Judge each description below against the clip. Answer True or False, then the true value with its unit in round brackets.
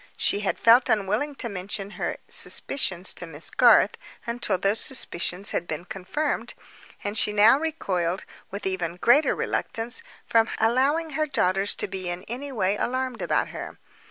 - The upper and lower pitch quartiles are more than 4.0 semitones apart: True (5.3 semitones)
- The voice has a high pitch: True (210 Hz)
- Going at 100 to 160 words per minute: True (155 wpm)